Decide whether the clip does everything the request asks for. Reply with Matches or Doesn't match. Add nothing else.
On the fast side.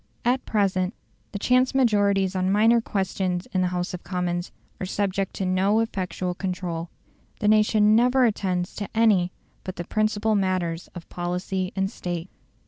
Doesn't match